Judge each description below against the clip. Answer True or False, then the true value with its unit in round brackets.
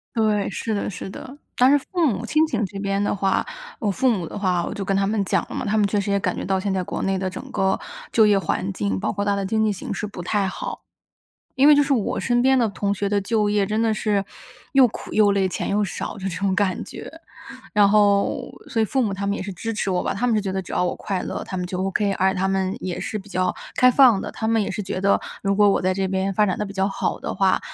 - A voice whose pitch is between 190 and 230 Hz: True (200 Hz)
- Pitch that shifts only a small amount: True (2.1 semitones)